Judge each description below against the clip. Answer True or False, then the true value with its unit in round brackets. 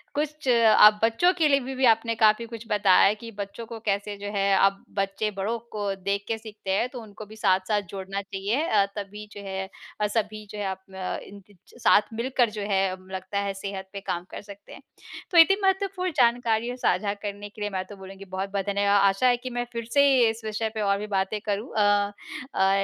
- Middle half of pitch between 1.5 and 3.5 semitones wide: True (2.7 semitones)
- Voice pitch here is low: False (210 Hz)